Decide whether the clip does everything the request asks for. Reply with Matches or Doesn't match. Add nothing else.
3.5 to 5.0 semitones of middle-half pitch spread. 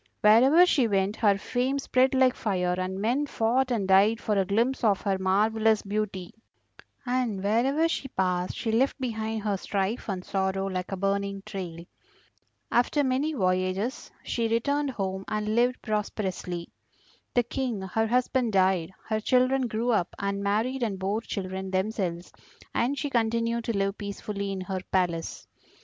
Matches